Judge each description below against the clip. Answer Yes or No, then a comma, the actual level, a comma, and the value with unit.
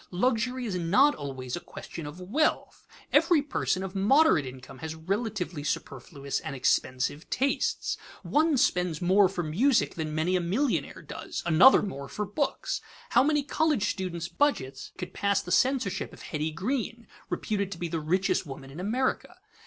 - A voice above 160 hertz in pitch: Yes, medium, 185 Hz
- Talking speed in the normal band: Yes, average, 160 wpm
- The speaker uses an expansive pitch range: Yes, wide, 8.0 semitones